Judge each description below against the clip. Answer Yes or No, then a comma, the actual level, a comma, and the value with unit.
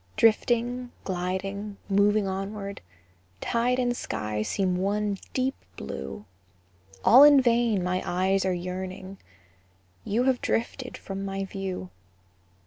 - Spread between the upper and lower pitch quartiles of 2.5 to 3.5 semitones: No, average, 4.0 semitones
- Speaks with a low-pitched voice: No, high, 195 Hz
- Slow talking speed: Yes, slow, 115 wpm